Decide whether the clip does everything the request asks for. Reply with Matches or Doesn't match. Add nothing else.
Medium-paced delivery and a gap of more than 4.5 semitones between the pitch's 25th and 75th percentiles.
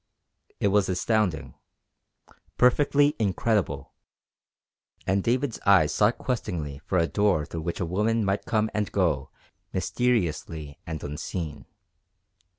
Doesn't match